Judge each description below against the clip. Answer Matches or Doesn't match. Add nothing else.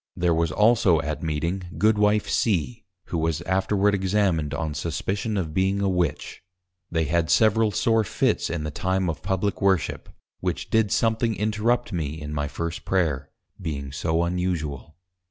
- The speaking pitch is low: Matches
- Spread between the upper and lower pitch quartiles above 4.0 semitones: Matches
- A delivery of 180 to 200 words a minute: Doesn't match